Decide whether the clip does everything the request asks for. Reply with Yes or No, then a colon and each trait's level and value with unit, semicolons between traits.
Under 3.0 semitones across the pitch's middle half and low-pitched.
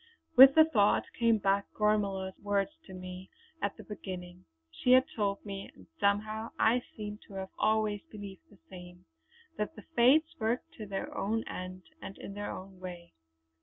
No: narrow, 2.6 semitones; high, 205 Hz